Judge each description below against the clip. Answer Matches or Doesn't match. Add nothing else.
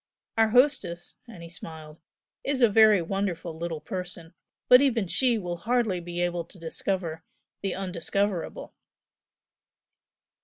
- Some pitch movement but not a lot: Matches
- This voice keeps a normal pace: Doesn't match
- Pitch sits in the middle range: Matches